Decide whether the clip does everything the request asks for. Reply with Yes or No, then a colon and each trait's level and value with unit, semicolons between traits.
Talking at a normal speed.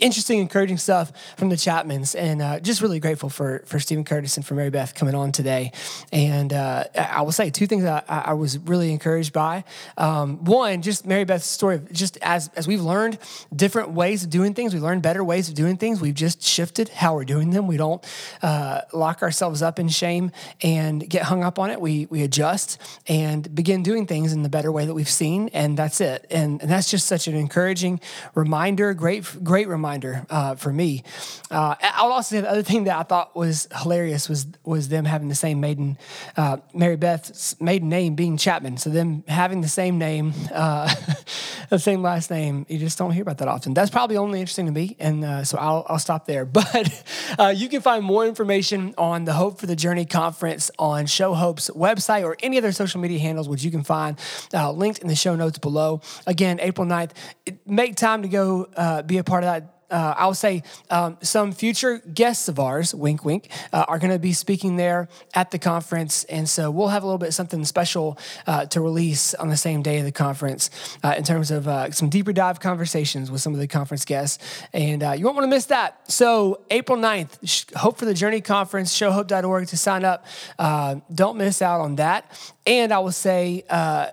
No: fast, 215 wpm